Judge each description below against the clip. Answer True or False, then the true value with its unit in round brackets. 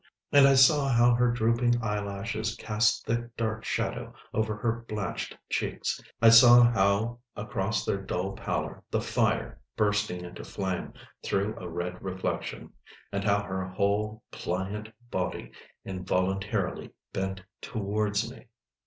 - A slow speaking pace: True (130 wpm)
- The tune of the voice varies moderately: True (3.1 semitones)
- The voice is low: True (105 Hz)